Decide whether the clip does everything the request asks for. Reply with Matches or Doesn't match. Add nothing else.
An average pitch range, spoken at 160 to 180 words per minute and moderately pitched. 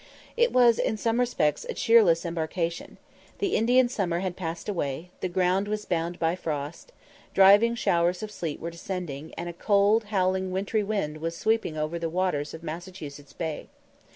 Matches